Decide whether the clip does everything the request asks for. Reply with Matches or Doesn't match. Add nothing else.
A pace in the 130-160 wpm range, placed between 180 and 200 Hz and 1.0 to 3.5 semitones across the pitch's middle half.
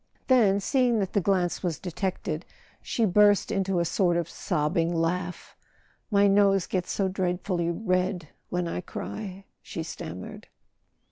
Matches